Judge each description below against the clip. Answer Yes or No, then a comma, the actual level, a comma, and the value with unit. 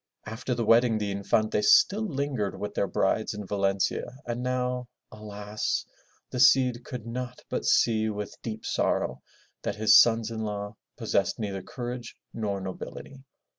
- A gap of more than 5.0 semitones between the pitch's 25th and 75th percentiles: No, average, 3.2 semitones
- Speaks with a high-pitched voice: No, low, 110 Hz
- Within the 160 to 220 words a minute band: No, average, 150 wpm